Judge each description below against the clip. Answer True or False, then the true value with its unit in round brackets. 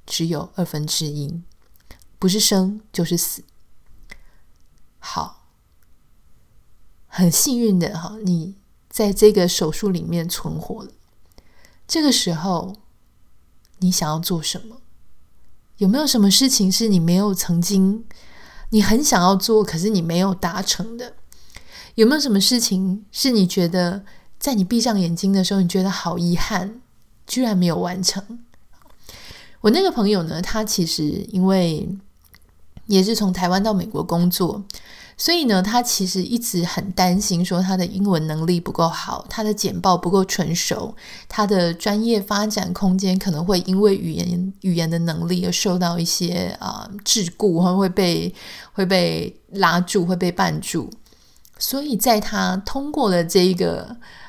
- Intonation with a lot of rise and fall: False (2.9 semitones)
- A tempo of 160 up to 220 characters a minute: True (215 characters per minute)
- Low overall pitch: False (190 Hz)